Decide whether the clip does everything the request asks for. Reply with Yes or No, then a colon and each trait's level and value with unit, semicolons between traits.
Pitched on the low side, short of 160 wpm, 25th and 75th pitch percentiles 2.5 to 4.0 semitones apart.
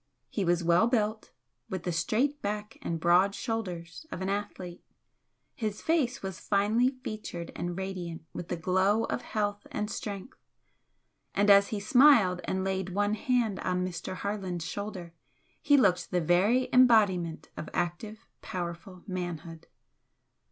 No: high, 195 Hz; average, 145 wpm; average, 3.5 semitones